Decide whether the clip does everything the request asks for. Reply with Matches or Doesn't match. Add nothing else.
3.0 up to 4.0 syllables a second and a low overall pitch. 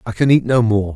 Doesn't match